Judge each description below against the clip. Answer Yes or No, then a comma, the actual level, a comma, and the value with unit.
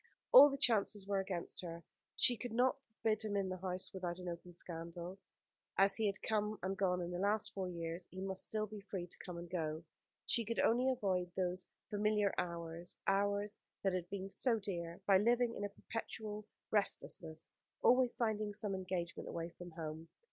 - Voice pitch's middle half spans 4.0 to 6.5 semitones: No, average, 3.3 semitones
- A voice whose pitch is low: No, high, 195 Hz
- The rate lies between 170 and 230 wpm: Yes, average, 185 wpm